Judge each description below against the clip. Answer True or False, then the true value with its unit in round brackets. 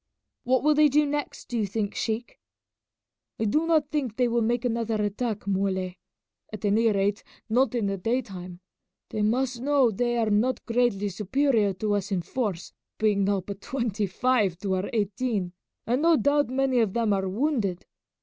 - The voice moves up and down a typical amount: True (4.2 semitones)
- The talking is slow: False (180 wpm)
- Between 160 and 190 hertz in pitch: False (225 Hz)